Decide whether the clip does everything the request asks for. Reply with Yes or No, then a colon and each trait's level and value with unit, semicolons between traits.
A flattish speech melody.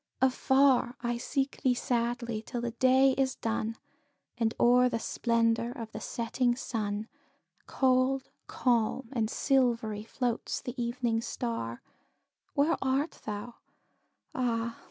Yes: narrow, 2.1 semitones